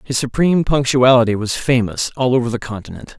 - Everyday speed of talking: Yes, average, 170 wpm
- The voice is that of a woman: No, male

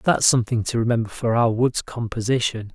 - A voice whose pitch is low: Yes, low, 115 Hz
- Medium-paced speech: Yes, average, 175 wpm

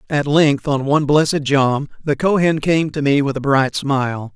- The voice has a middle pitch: Yes, medium, 145 Hz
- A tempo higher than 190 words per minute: Yes, fast, 205 wpm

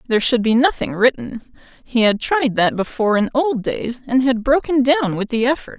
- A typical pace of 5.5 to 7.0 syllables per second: No, 5.1 syllables/s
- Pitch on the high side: Yes, high, 245 Hz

